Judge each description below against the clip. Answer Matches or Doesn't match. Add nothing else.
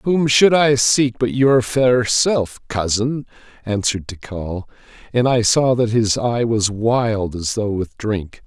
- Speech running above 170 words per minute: Doesn't match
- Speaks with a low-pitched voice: Matches